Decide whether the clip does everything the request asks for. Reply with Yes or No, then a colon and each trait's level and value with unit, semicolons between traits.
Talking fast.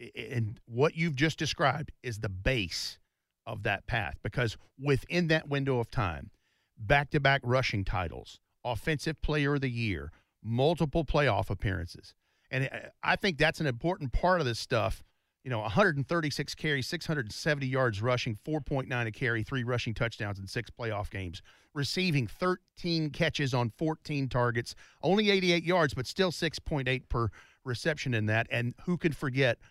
No: average, 150 wpm